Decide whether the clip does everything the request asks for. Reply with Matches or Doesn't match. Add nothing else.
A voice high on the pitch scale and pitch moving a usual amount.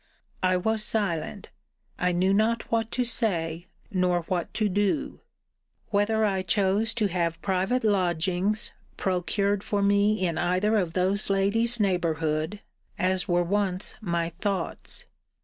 Matches